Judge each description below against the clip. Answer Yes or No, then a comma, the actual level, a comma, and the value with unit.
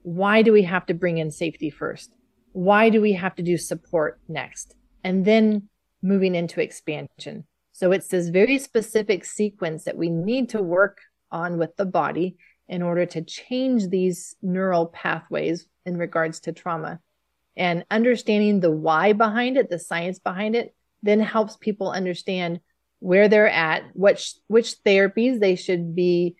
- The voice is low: No, medium, 185 Hz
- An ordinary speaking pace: Yes, average, 160 wpm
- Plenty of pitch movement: No, average, 3.5 semitones